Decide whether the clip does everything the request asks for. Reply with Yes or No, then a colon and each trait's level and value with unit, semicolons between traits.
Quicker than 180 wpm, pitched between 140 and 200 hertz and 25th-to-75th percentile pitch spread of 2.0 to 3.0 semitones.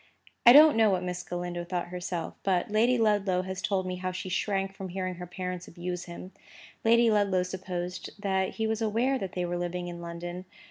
Yes: average, 200 wpm; medium, 185 Hz; narrow, 2.4 semitones